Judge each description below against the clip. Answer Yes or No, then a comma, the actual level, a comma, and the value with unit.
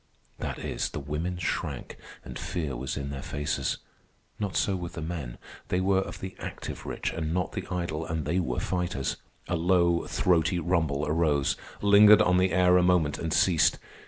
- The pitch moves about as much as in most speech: Yes, average, 3.2 semitones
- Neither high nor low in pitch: No, very low, 85 Hz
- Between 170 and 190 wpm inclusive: Yes, average, 185 wpm